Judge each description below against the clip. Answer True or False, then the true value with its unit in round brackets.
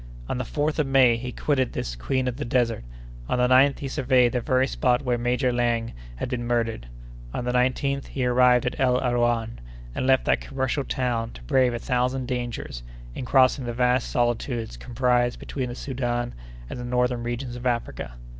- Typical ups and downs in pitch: False (1.3 semitones)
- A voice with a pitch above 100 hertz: True (125 Hz)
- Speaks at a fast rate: False (190 wpm)